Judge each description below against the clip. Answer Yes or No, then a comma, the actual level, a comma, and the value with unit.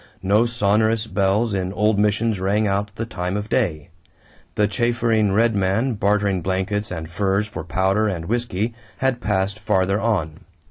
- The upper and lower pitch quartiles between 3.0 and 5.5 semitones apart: No, narrow, 2.5 semitones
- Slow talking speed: No, average, 155 wpm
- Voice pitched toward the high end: No, low, 100 Hz